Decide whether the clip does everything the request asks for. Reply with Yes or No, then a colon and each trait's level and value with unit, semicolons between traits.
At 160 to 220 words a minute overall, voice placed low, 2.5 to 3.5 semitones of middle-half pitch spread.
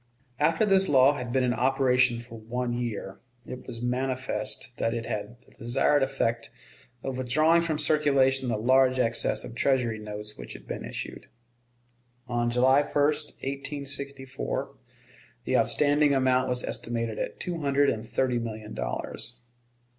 No: average, 145 wpm; low, 130 Hz; average, 2.8 semitones